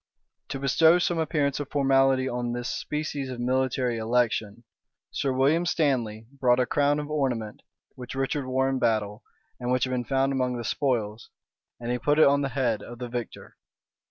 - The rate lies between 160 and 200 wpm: Yes, average, 185 wpm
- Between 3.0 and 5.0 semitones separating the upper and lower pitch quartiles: No, narrow, 2.5 semitones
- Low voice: Yes, low, 130 Hz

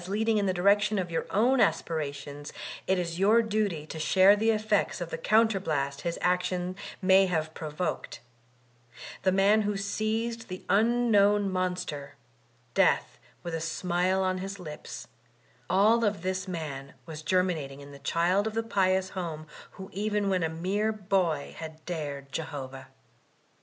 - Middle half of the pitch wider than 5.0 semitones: No, average, 4.1 semitones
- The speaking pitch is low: No, medium, 185 Hz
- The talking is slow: No, average, 155 wpm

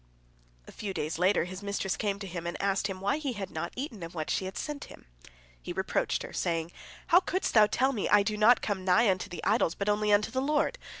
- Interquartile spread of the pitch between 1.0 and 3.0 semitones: No, average, 3.6 semitones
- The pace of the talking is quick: Yes, fast, 245 wpm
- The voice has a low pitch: No, high, 200 Hz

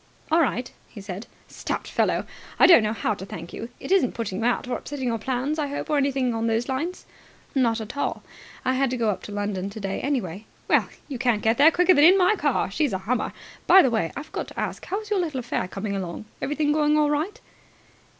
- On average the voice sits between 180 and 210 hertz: No, very high, 250 Hz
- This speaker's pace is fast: Yes, fast, 235 wpm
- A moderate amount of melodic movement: No, wide, 5.8 semitones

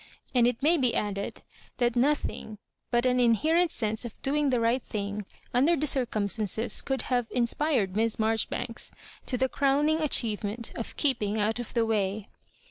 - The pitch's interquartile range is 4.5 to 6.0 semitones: No, average, 3.6 semitones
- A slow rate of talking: No, average, 160 wpm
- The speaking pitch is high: Yes, high, 240 Hz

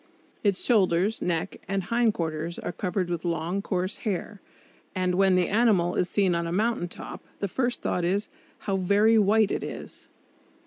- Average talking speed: Yes, average, 170 wpm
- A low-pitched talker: No, high, 190 Hz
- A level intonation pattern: No, average, 3.0 semitones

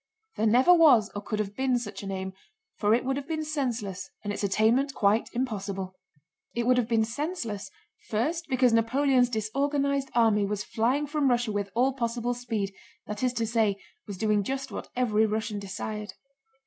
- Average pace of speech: Yes, average, 180 wpm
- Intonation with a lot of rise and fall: No, average, 3.9 semitones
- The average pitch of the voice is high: Yes, high, 230 Hz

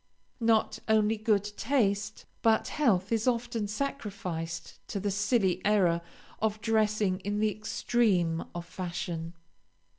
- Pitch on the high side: Yes, high, 210 Hz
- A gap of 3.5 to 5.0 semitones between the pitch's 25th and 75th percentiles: No, average, 3.1 semitones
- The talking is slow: Yes, slow, 120 wpm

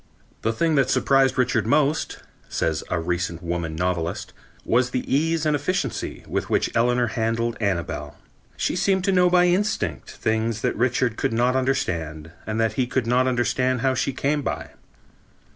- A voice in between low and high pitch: No, low, 125 Hz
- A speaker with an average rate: Yes, average, 170 wpm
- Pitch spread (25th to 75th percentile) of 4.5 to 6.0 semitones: Yes, average, 5.3 semitones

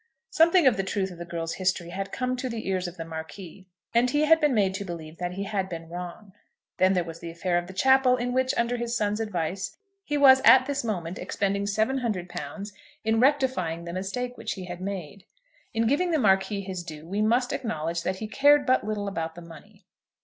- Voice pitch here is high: Yes, high, 200 Hz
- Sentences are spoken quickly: Yes, fast, 220 wpm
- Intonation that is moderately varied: No, wide, 6.0 semitones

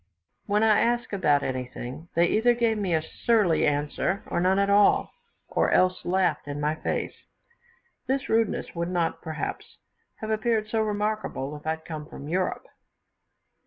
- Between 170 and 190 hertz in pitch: Yes, medium, 185 Hz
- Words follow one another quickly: No, average, 160 wpm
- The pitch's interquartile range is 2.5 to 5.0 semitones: No, wide, 5.4 semitones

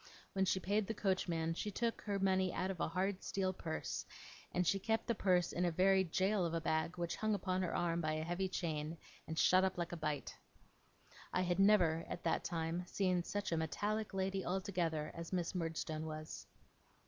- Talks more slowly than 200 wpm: No, fast, 205 wpm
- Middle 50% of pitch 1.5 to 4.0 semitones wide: Yes, average, 2.7 semitones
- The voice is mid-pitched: Yes, medium, 180 Hz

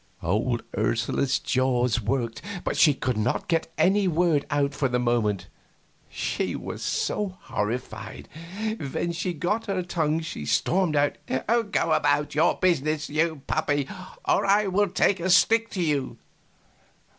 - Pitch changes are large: Yes, wide, 5.7 semitones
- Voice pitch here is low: No, medium, 150 Hz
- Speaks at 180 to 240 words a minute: No, average, 145 wpm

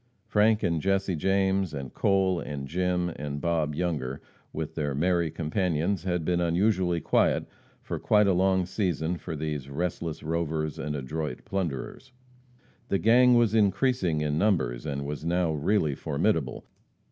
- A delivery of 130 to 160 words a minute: Yes, average, 145 wpm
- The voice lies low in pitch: Yes, very low, 85 Hz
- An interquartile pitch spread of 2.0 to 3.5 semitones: No, average, 4.2 semitones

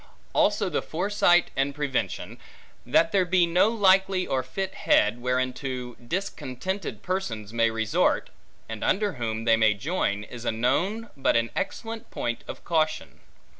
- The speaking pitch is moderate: Yes, medium, 145 Hz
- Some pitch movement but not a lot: No, wide, 8.1 semitones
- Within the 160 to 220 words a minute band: No, average, 145 wpm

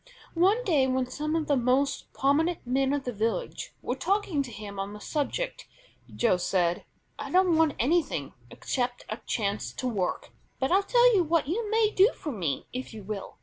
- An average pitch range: No, wide, 7.6 semitones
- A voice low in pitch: No, very high, 275 Hz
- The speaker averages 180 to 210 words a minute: Yes, average, 190 wpm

